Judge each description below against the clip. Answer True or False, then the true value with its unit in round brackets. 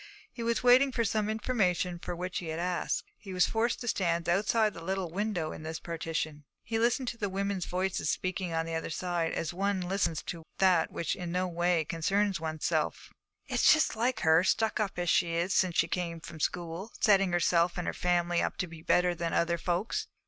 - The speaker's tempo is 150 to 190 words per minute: False (205 wpm)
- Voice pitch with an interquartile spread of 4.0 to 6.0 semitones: False (3.2 semitones)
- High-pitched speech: False (180 Hz)